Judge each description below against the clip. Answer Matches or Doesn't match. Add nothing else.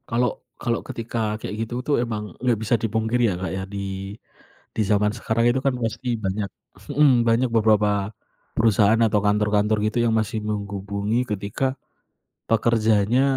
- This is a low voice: Matches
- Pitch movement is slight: Matches